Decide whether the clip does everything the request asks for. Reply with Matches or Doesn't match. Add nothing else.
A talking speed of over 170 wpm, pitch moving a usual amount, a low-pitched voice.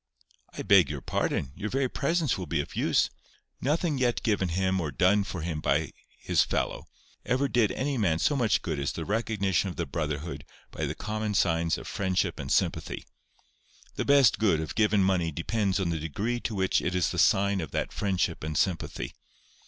Matches